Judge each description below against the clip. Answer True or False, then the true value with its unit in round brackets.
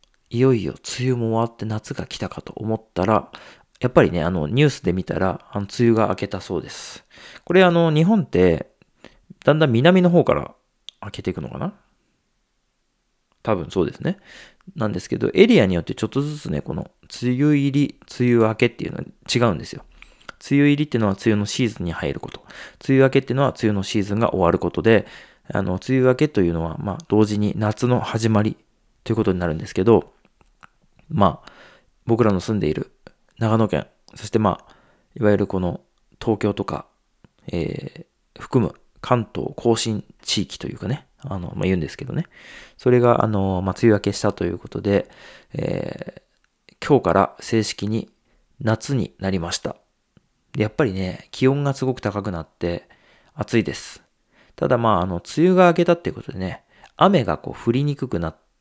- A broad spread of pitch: False (4.5 semitones)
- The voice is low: True (110 Hz)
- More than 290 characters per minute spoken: True (350 characters per minute)